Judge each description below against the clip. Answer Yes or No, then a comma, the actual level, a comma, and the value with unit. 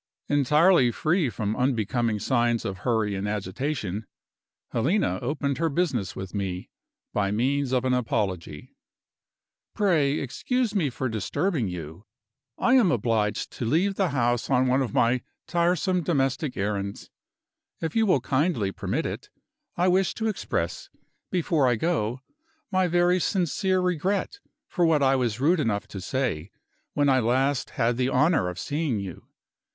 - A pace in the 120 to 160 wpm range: Yes, average, 150 wpm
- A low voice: Yes, low, 130 Hz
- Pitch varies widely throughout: Yes, wide, 7.4 semitones